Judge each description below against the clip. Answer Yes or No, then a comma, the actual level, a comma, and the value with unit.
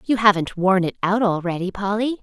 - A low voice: No, high, 200 Hz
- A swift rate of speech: No, average, 190 wpm